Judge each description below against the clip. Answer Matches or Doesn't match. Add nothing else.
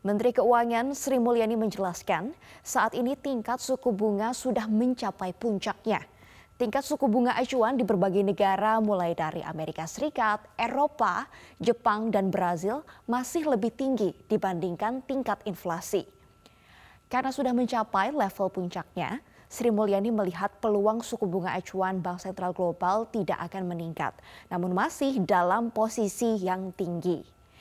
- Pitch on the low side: Doesn't match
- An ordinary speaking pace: Matches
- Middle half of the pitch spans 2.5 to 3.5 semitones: Doesn't match